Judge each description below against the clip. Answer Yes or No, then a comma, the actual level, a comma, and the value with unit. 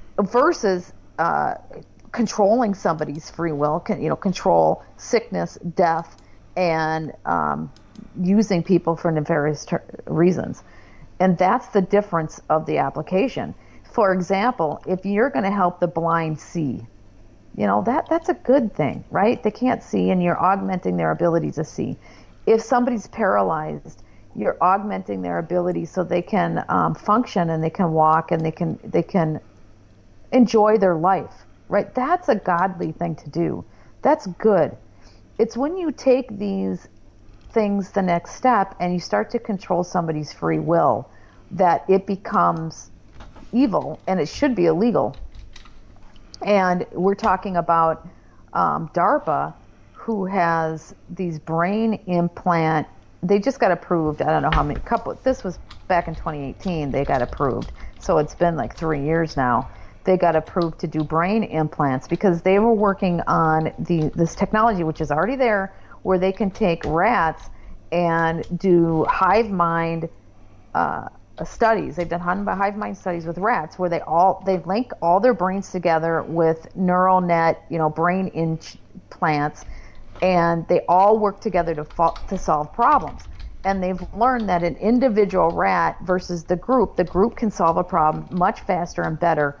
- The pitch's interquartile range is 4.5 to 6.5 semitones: No, average, 3.9 semitones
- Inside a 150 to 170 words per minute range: Yes, average, 155 wpm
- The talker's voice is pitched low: No, medium, 175 Hz